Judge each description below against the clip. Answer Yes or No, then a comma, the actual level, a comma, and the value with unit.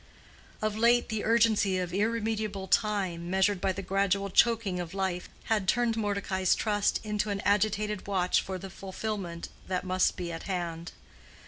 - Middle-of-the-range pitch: No, high, 195 Hz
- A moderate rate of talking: Yes, average, 155 wpm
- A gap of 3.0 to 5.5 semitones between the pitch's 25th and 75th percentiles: No, narrow, 2.5 semitones